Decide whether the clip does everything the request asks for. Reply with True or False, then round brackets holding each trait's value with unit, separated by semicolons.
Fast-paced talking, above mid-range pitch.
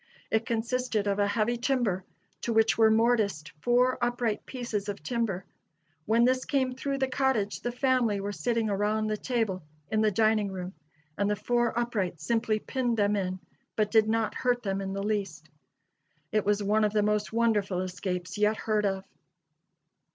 False (175 wpm; 215 Hz)